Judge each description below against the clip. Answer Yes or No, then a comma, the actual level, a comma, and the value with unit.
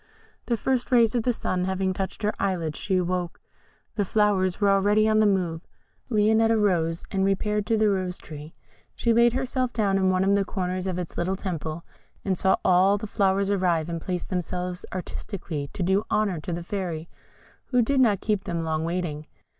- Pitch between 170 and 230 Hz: Yes, high, 190 Hz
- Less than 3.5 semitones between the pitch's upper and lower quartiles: Yes, average, 2.9 semitones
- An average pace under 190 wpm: No, average, 195 wpm